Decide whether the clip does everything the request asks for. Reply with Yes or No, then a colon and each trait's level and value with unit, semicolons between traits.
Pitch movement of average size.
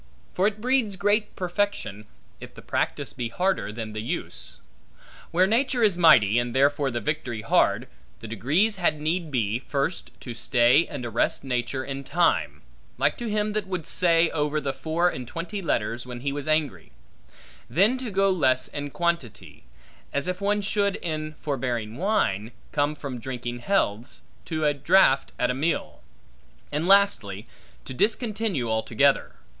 No: wide, 7.6 semitones